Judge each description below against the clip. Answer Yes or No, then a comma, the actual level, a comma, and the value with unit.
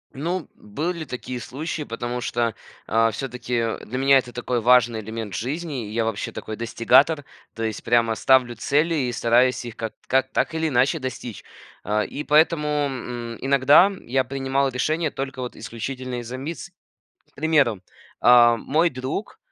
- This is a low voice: Yes, low, 130 Hz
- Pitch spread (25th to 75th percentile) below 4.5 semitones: Yes, average, 3.5 semitones